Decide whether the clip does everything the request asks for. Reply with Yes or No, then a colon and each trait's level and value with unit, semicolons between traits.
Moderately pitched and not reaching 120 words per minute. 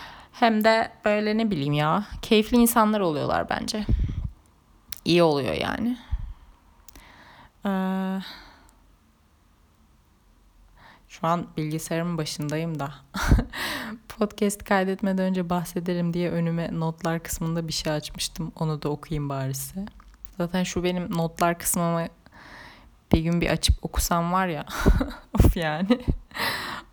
Yes: medium, 170 Hz; average, 110 wpm